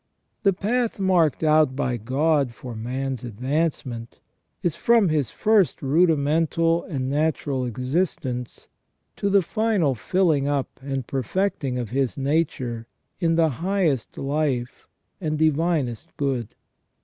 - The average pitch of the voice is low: No, medium, 145 Hz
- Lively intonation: No, average, 4.6 semitones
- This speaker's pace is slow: Yes, slow, 120 wpm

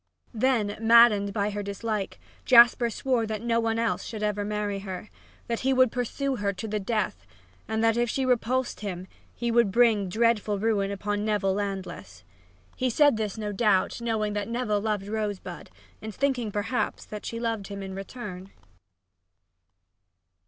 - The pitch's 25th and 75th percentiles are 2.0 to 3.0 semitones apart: Yes, narrow, 2.6 semitones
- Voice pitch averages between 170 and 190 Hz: No, high, 215 Hz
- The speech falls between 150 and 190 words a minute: Yes, average, 165 wpm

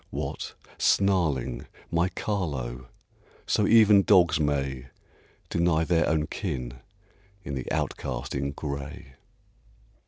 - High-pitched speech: No, very low, 75 Hz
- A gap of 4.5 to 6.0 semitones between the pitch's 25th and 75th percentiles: Yes, average, 5.2 semitones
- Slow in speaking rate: Yes, slow, 100 wpm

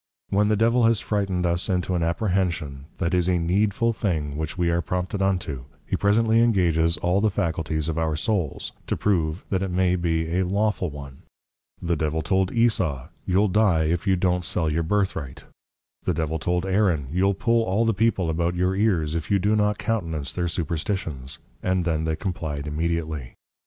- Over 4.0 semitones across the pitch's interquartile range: No, average, 3.7 semitones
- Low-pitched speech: Yes, very low, 90 Hz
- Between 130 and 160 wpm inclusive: No, average, 190 wpm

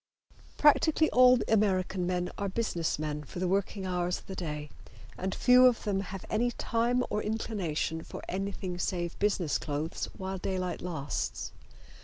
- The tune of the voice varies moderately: Yes, average, 3.4 semitones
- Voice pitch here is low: No, high, 190 Hz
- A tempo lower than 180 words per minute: Yes, average, 155 wpm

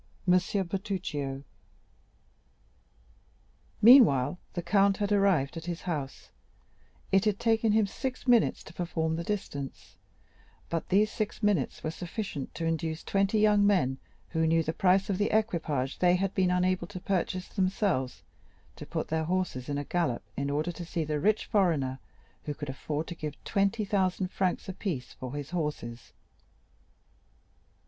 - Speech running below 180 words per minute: Yes, average, 150 wpm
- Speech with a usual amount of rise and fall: Yes, average, 4.6 semitones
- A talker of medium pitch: Yes, medium, 180 Hz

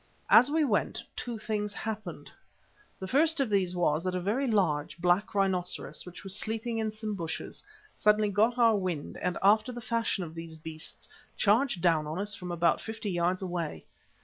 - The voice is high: Yes, high, 200 Hz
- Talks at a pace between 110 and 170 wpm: No, average, 180 wpm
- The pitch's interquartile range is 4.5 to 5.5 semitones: No, average, 4.0 semitones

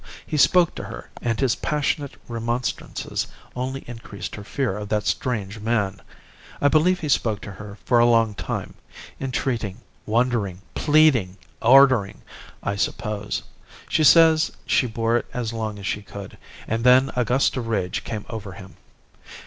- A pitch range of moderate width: Yes, average, 4.2 semitones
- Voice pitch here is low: Yes, low, 115 Hz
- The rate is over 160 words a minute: No, average, 155 wpm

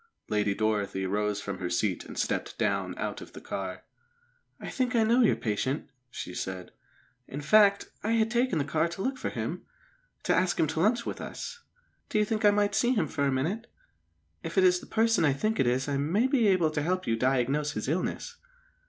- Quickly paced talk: Yes, fast, 215 wpm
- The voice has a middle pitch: Yes, medium, 160 Hz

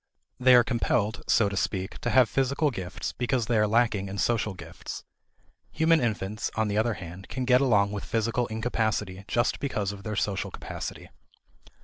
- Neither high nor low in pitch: No, low, 110 Hz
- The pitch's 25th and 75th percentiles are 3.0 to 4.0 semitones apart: Yes, average, 3.3 semitones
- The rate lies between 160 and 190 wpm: Yes, average, 175 wpm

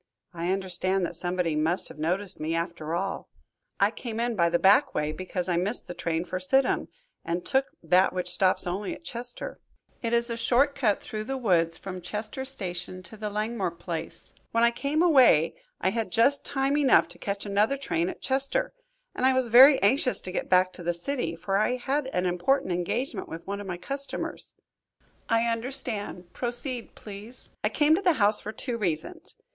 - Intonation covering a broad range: Yes, wide, 6.0 semitones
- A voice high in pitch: Yes, high, 205 Hz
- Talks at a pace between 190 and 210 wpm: Yes, average, 195 wpm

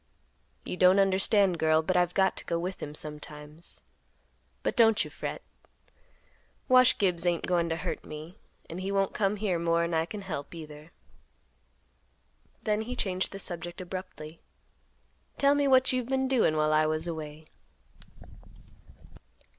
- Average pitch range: Yes, average, 3.9 semitones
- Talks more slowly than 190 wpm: Yes, average, 150 wpm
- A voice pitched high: No, medium, 180 Hz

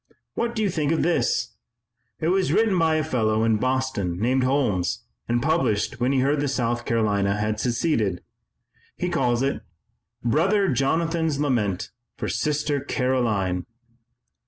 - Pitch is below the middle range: Yes, low, 130 Hz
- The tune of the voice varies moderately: No, wide, 6.2 semitones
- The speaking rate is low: No, average, 145 wpm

